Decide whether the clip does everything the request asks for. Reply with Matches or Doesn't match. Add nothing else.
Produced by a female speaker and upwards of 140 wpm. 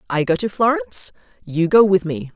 Matches